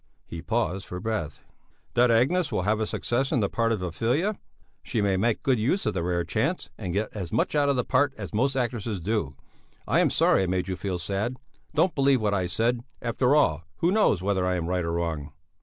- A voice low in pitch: Yes, low, 110 Hz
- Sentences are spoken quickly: Yes, fast, 225 wpm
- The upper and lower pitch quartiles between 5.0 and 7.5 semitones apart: Yes, wide, 5.4 semitones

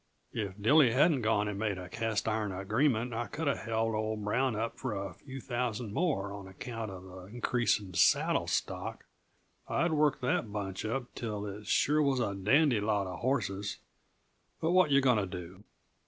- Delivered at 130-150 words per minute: No, average, 185 wpm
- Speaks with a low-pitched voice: Yes, low, 110 Hz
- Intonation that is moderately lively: Yes, average, 4.3 semitones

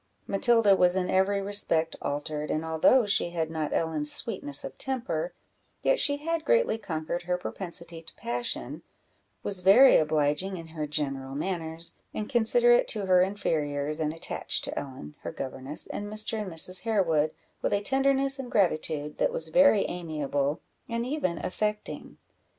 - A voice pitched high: No, medium, 180 Hz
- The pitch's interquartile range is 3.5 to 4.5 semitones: No, wide, 5.6 semitones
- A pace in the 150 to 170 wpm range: Yes, average, 155 wpm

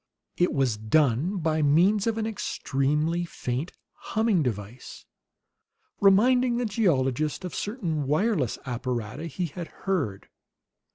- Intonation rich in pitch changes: Yes, wide, 6.9 semitones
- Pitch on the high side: No, medium, 160 Hz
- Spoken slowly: Yes, slow, 115 wpm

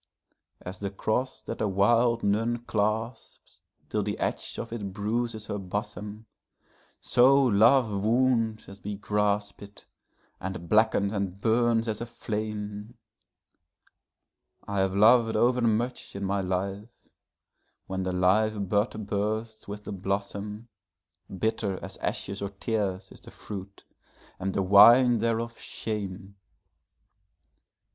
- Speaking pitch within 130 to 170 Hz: No, low, 105 Hz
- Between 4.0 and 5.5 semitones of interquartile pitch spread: No, narrow, 2.4 semitones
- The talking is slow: Yes, slow, 120 wpm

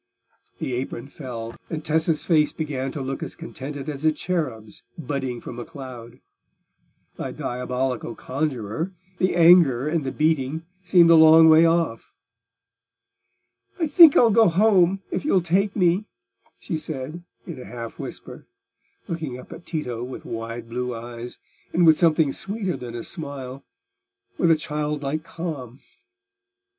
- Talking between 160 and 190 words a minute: No, average, 145 wpm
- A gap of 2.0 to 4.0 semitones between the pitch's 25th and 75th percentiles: No, average, 5.0 semitones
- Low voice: No, medium, 150 Hz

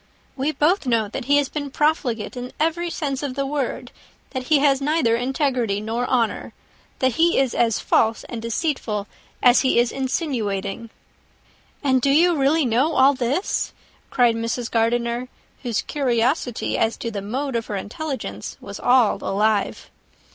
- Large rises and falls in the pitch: No, average, 3.8 semitones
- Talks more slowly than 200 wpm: Yes, average, 160 wpm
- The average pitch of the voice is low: No, very high, 255 Hz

